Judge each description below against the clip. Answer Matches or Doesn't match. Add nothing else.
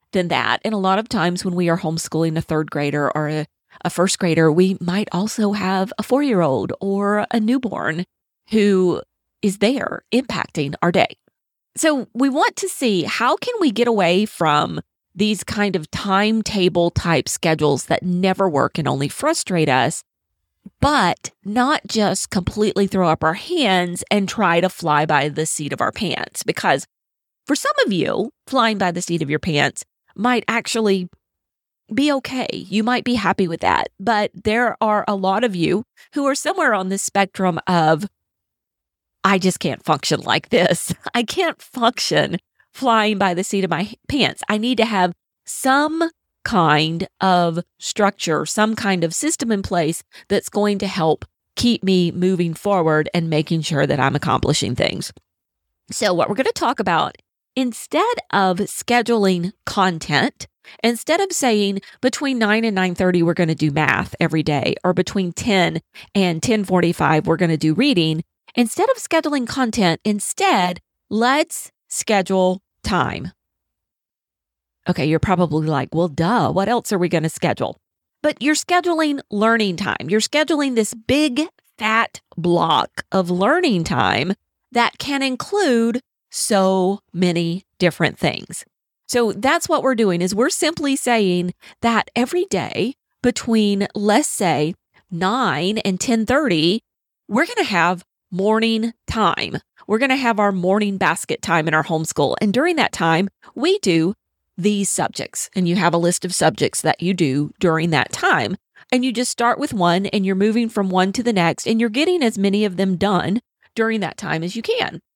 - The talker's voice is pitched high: Matches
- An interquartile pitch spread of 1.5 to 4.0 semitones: Doesn't match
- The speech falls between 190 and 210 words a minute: Doesn't match